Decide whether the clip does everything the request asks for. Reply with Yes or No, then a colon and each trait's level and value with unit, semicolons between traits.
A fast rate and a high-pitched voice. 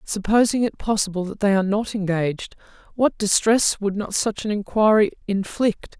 No: average, 160 wpm; high, 205 Hz